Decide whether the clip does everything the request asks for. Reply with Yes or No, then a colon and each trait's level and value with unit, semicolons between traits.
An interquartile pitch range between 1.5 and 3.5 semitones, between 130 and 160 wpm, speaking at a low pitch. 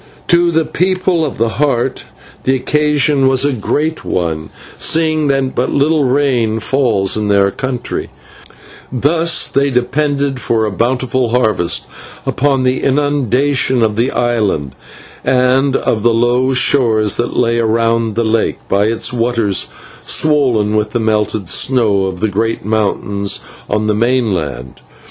No: average, 4.2 semitones; average, 145 wpm; low, 120 Hz